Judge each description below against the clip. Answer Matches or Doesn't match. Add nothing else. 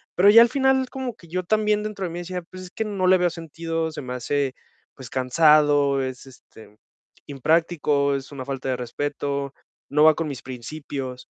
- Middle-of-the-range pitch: Matches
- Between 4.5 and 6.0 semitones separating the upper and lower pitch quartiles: Matches